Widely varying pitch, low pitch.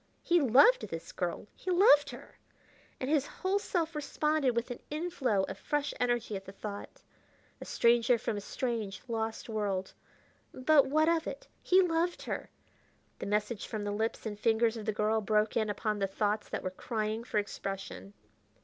No: wide, 6.0 semitones; high, 230 Hz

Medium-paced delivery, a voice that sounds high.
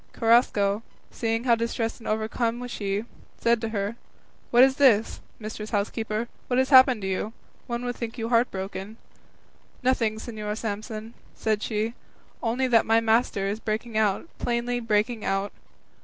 Yes: average, 155 wpm; high, 225 Hz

